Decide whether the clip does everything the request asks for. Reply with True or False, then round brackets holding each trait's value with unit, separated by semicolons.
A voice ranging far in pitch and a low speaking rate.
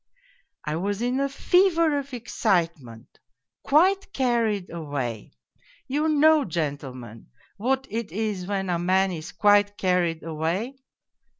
True (8.3 semitones; 120 wpm)